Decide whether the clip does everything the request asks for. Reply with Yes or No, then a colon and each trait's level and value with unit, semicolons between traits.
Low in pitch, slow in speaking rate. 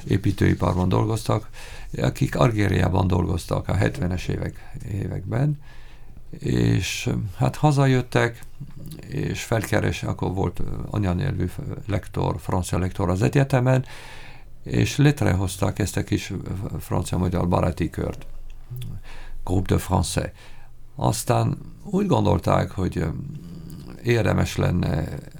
Yes: low, 105 Hz; slow, 90 wpm